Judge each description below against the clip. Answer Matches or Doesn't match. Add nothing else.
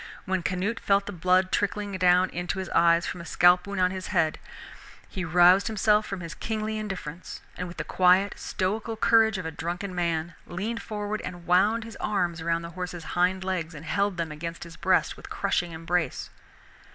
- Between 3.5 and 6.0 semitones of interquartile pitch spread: Doesn't match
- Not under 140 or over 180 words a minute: Doesn't match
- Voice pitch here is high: Doesn't match